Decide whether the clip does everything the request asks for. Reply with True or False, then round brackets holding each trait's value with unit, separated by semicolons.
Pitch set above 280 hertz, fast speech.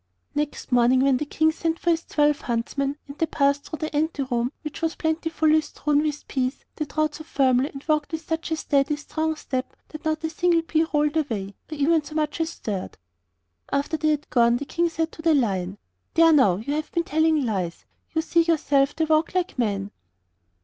True (300 Hz; 210 wpm)